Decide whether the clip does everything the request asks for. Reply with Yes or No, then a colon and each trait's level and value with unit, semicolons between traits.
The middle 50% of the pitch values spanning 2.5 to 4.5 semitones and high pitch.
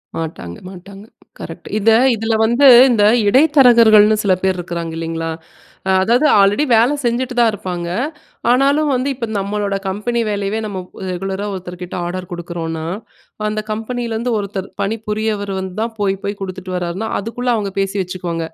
Yes: average, 3.7 semitones; high, 205 Hz